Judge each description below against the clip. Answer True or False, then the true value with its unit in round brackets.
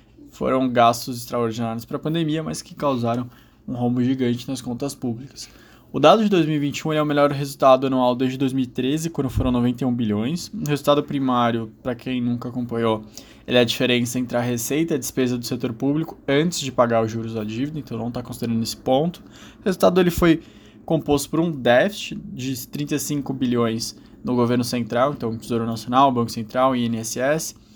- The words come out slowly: False (180 wpm)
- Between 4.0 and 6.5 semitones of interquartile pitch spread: False (3.4 semitones)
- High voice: False (125 Hz)